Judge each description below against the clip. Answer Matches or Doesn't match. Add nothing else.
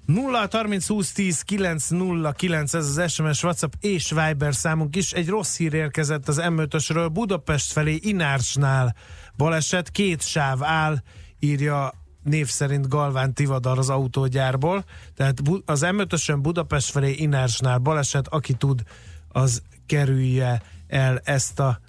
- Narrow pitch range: Doesn't match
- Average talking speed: Matches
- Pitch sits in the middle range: Matches